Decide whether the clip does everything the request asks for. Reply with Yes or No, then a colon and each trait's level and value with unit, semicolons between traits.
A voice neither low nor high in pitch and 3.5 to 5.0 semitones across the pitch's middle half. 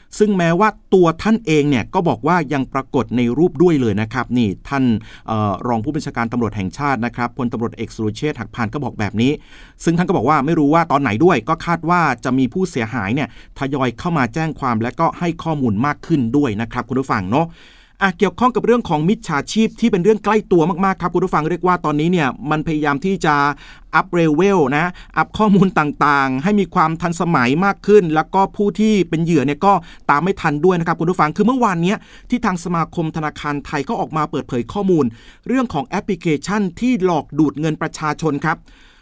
No: medium, 160 Hz; wide, 5.4 semitones